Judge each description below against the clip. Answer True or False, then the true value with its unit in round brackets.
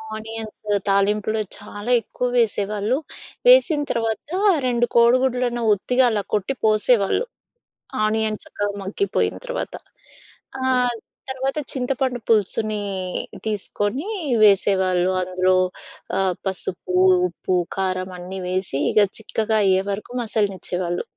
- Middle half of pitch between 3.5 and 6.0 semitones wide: True (4.0 semitones)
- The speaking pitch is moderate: False (215 Hz)